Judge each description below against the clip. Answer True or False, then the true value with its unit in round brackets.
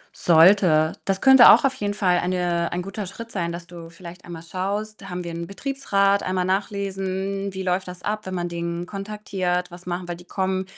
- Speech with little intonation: True (2.2 semitones)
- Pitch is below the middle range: False (185 Hz)